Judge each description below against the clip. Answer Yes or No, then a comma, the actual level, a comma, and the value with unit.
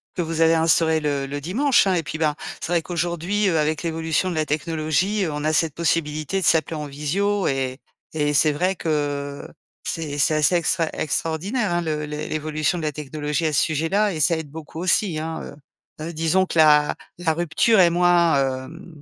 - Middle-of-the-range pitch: Yes, medium, 160 Hz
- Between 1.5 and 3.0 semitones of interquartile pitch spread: Yes, narrow, 2.4 semitones